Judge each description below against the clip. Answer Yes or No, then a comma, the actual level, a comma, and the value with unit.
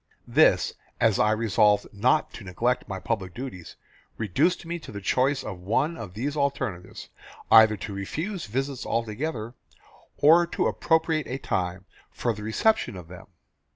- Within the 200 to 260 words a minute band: No, average, 155 wpm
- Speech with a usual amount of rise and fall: No, wide, 6.3 semitones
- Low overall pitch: Yes, low, 115 Hz